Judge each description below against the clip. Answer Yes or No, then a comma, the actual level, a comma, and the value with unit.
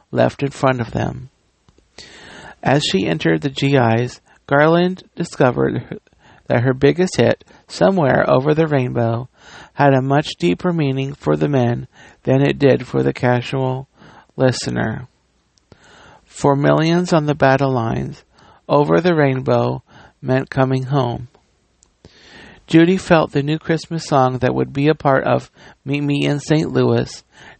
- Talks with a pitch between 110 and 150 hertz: Yes, low, 135 Hz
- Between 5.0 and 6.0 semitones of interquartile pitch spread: No, average, 3.2 semitones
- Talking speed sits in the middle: Yes, average, 145 wpm